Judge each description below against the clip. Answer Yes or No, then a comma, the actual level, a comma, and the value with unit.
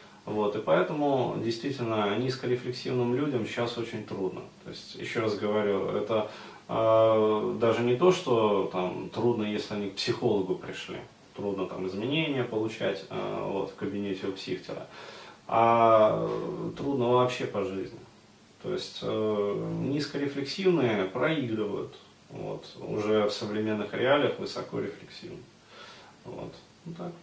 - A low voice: Yes, low, 110 Hz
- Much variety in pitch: No, average, 3.3 semitones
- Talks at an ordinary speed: Yes, average, 125 wpm